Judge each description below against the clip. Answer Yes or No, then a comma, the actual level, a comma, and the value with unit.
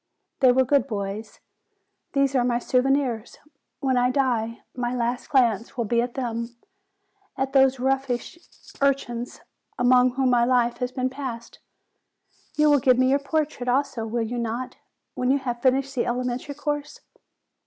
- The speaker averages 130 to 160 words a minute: Yes, average, 155 wpm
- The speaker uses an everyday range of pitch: No, narrow, 2.1 semitones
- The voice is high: Yes, very high, 250 Hz